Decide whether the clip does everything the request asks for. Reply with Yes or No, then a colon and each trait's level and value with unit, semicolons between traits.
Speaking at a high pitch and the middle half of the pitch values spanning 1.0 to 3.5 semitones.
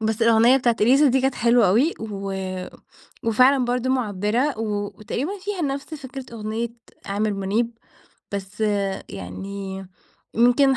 No: high, 230 Hz; average, 4.2 semitones